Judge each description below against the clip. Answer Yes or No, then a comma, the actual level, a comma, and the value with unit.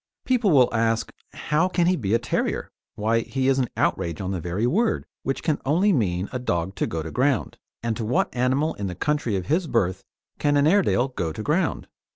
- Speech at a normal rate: No, fast, 215 wpm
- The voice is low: Yes, low, 125 Hz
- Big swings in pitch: Yes, wide, 6.9 semitones